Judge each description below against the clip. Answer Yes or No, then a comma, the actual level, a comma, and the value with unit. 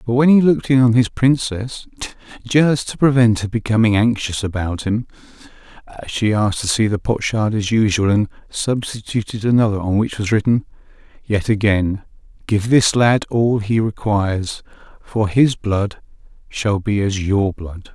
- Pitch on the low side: Yes, low, 110 Hz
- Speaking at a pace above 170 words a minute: No, average, 155 wpm